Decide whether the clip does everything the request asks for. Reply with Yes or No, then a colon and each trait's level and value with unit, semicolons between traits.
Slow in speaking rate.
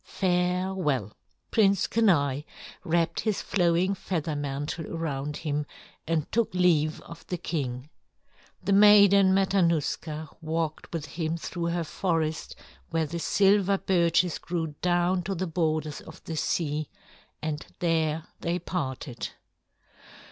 Yes: slow, 120 wpm